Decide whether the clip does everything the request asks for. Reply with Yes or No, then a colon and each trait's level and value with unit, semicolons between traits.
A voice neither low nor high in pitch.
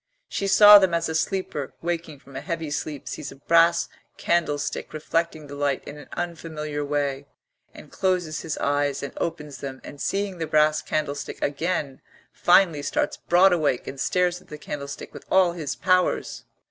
Yes: medium, 155 Hz